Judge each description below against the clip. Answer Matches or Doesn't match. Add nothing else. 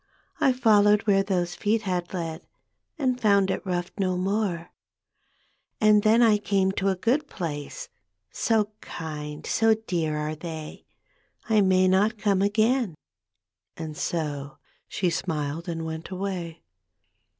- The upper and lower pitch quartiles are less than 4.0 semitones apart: Doesn't match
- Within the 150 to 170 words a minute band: Doesn't match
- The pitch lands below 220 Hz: Matches